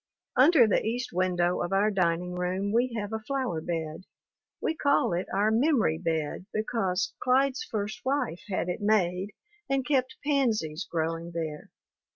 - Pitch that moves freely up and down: Yes, wide, 6.2 semitones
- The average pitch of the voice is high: Yes, high, 200 Hz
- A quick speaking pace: No, average, 155 wpm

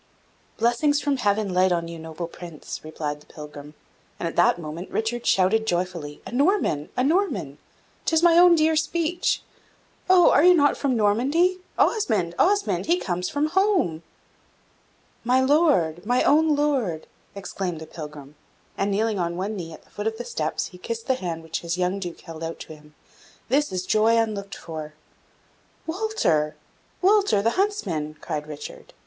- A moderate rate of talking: Yes, average, 165 wpm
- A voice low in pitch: No, high, 205 Hz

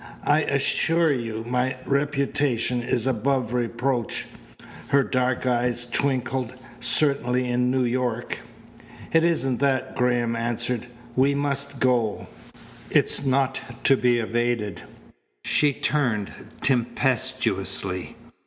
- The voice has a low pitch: Yes, low, 125 Hz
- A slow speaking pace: Yes, slow, 105 wpm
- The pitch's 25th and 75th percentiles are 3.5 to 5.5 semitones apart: No, narrow, 2.5 semitones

